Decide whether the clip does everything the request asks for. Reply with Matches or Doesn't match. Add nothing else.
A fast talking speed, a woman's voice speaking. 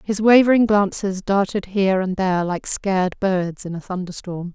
Doesn't match